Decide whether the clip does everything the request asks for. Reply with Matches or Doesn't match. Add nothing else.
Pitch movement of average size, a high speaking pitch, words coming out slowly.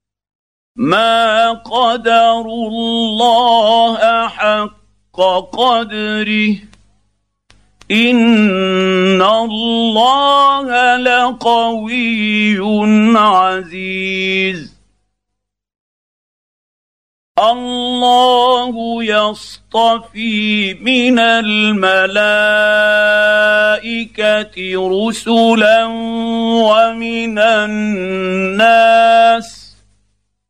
Matches